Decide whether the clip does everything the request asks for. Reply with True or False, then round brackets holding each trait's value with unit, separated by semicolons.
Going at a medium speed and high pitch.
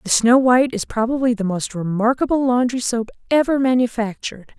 True (155 wpm; 240 Hz)